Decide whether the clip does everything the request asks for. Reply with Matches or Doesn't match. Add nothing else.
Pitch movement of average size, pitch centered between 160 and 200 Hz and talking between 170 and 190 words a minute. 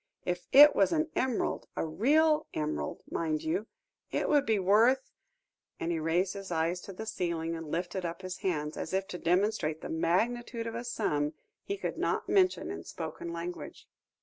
Doesn't match